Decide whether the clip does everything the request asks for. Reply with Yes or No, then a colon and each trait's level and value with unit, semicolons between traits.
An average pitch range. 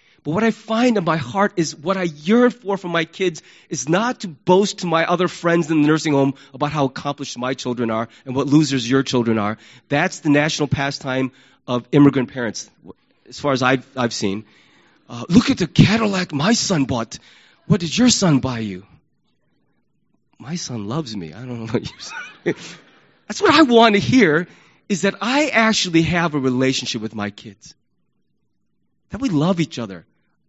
No: wide, 6.5 semitones